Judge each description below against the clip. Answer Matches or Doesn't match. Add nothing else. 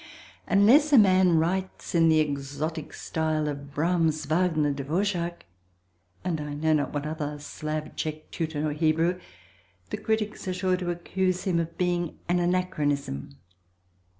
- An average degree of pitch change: Matches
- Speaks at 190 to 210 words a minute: Doesn't match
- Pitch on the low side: Doesn't match